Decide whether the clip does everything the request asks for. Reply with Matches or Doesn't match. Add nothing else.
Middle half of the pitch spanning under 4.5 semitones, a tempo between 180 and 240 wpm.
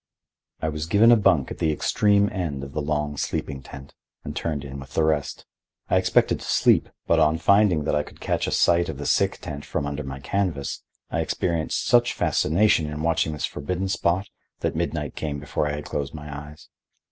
Matches